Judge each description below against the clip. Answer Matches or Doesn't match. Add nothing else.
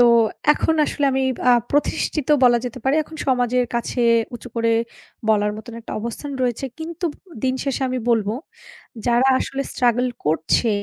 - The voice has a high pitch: Matches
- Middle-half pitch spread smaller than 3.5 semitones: Matches